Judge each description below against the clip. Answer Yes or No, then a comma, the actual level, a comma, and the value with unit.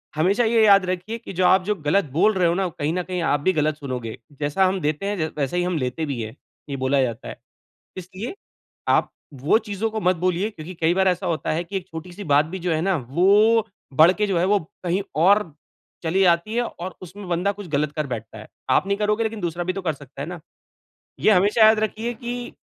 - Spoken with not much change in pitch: No, average, 4.4 semitones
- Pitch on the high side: No, medium, 180 Hz